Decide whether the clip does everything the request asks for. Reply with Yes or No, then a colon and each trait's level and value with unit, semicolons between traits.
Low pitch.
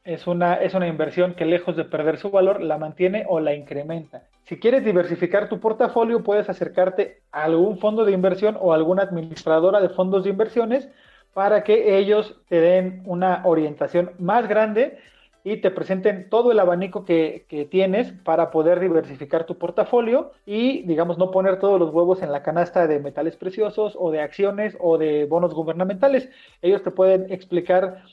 No: medium, 185 Hz